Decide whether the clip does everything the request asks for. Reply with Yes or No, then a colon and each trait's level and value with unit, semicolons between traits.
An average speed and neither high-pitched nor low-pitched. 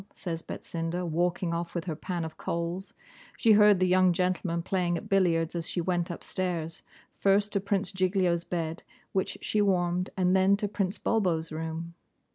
Yes: average, 170 wpm; medium, 180 Hz